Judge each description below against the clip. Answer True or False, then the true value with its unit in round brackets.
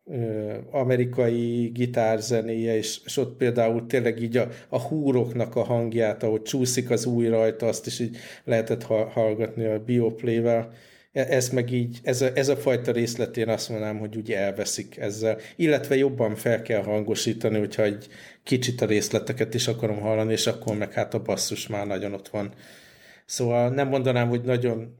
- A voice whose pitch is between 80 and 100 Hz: False (115 Hz)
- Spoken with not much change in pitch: True (2.0 semitones)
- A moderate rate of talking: False (170 wpm)